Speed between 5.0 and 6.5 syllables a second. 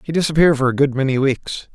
No: 6.9 syllables/s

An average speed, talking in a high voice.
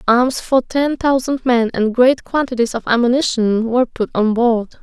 Yes: average, 175 wpm; high, 240 Hz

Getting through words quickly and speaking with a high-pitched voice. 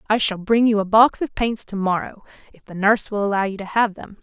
Yes: fast, 270 wpm; high, 210 Hz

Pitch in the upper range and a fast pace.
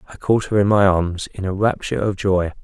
No: very low, 95 Hz; fast, 250 wpm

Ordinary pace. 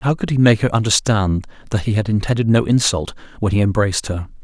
No: fast, 215 wpm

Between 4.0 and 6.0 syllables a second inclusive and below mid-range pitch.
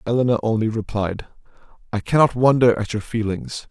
Yes: 5.4 syllables/s; low, 115 Hz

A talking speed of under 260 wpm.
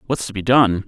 No: fast, 275 wpm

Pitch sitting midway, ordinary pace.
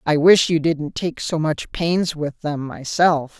Yes: medium, 160 Hz; average, 195 wpm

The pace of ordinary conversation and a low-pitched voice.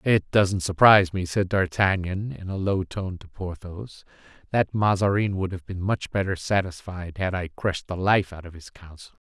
Yes: average, 190 wpm; very low, 95 Hz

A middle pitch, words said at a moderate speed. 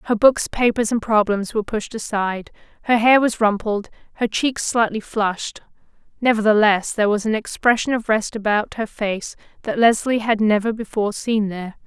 No: high, 215 Hz; average, 165 wpm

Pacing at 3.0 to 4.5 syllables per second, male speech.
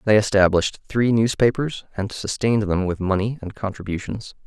No: 5.4 syllables/s; male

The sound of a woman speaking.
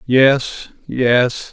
No: male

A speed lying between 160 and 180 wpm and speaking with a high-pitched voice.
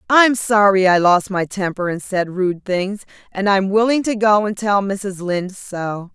No: average, 195 wpm; high, 195 Hz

